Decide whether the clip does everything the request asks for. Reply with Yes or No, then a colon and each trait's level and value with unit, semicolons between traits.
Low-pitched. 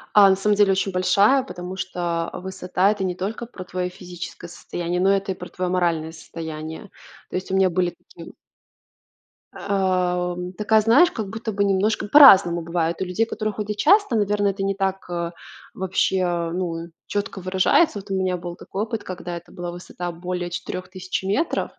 No: medium, 185 Hz